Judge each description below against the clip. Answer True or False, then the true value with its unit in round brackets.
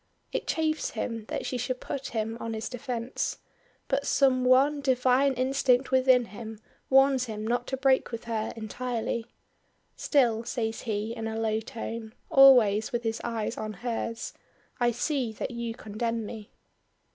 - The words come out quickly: False (155 wpm)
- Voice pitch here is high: True (235 Hz)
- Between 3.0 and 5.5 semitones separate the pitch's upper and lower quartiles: False (2.6 semitones)